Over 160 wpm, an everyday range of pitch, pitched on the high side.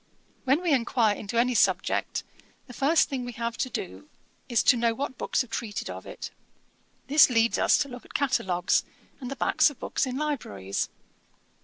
Yes: average, 185 wpm; average, 3.2 semitones; very high, 250 Hz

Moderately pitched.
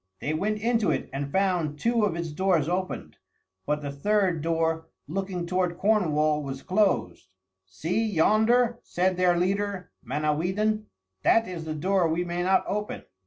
Yes: medium, 180 Hz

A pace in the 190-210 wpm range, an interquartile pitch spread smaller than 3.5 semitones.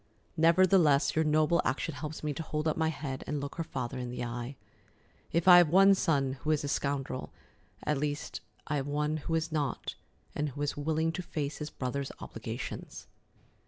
Yes: average, 195 wpm; narrow, 2.4 semitones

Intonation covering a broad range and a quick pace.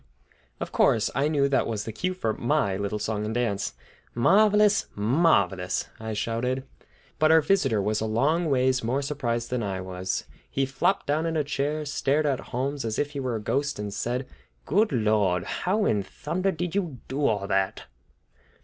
No: wide, 5.9 semitones; average, 185 wpm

